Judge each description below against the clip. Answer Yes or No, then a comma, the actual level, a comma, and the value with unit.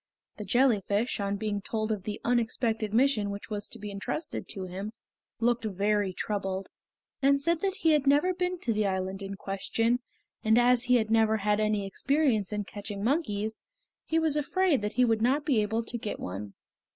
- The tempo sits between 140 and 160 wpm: No, average, 190 wpm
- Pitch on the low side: No, high, 220 Hz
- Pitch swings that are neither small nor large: Yes, average, 3.8 semitones